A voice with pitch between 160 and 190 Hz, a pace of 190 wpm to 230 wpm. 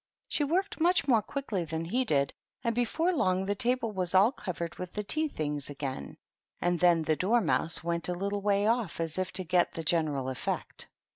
Yes: medium, 185 Hz; average, 200 wpm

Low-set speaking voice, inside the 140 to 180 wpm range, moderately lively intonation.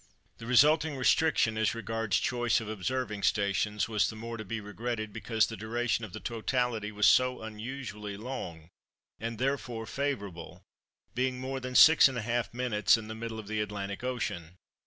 Yes: low, 115 Hz; average, 160 wpm; average, 3.0 semitones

